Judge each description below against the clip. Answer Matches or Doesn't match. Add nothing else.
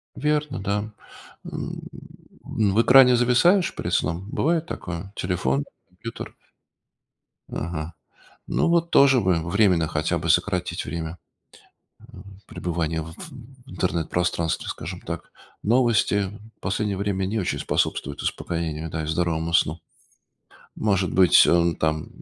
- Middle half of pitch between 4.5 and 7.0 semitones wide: Matches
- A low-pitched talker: Matches